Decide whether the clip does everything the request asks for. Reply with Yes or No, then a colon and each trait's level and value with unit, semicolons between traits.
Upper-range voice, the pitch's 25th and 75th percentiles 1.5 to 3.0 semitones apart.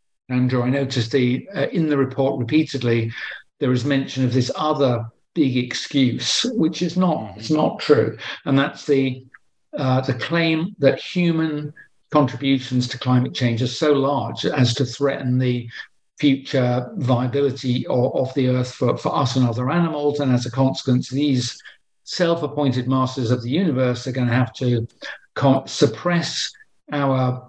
No: low, 135 Hz; narrow, 2.6 semitones